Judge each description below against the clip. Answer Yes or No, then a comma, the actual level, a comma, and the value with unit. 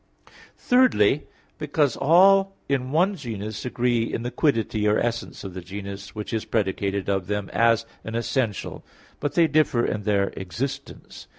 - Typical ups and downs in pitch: No, wide, 5.7 semitones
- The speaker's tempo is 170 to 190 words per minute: No, average, 155 wpm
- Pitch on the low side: Yes, low, 115 Hz